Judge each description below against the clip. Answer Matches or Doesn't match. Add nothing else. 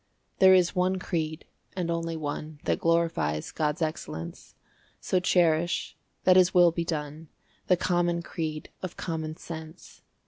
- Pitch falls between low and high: Matches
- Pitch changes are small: Matches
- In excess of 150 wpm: Doesn't match